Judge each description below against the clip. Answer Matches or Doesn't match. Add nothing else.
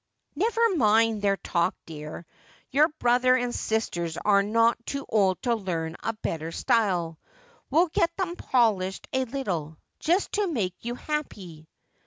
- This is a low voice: Doesn't match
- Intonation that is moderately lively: Doesn't match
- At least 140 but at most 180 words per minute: Matches